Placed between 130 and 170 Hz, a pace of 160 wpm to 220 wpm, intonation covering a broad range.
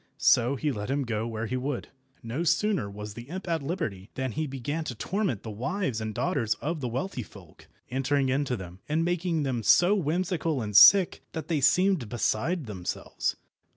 Yes: low, 135 Hz; average, 190 wpm; wide, 6.8 semitones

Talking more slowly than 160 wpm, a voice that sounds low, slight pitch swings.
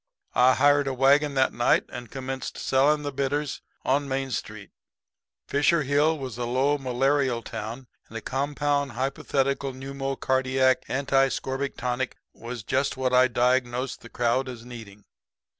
Yes: average, 145 wpm; low, 130 Hz; narrow, 2.0 semitones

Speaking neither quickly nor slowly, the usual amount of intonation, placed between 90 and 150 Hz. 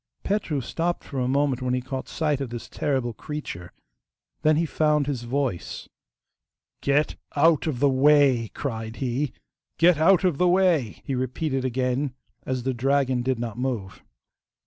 Yes: average, 160 wpm; average, 3.2 semitones; low, 135 Hz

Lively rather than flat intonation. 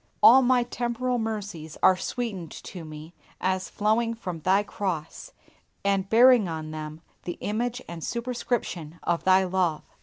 Yes: wide, 5.8 semitones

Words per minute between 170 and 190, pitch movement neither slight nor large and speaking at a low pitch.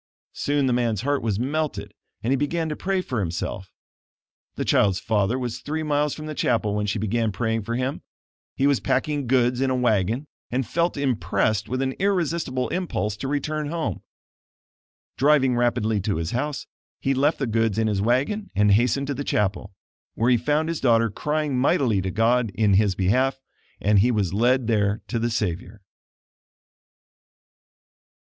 Yes: average, 175 wpm; average, 5.0 semitones; low, 120 Hz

